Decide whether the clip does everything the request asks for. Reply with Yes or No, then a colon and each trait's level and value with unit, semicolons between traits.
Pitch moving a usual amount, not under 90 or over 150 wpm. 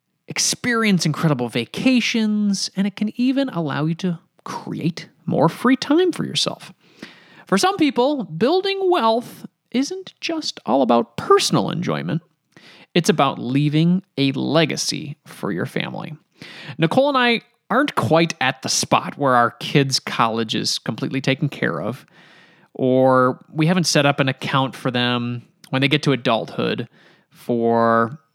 No: wide, 7.8 semitones; average, 140 wpm